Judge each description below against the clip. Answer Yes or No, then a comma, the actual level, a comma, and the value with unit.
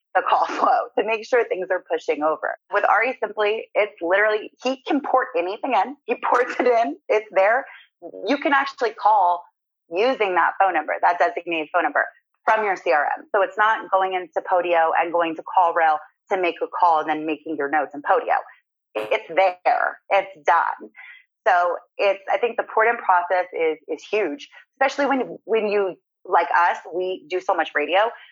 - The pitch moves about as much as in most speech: No, wide, 5.8 semitones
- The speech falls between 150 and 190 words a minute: Yes, average, 185 wpm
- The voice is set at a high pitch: Yes, high, 195 Hz